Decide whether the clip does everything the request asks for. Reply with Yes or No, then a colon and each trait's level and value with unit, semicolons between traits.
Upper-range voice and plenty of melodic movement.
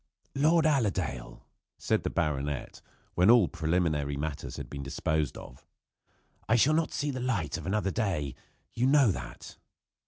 No: very low, 90 Hz; wide, 9.0 semitones